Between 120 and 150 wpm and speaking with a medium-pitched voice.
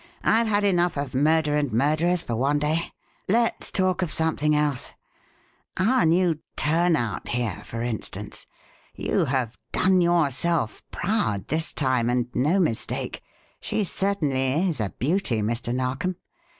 Yes: slow, 135 wpm; medium, 150 Hz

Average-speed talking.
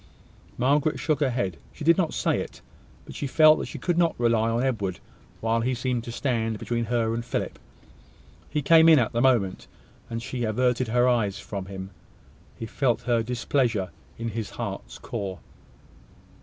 Yes: average, 180 wpm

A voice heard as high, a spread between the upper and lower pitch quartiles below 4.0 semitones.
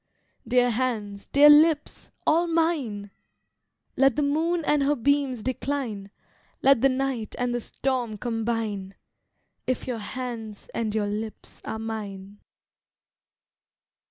No: high, 245 Hz; average, 4.5 semitones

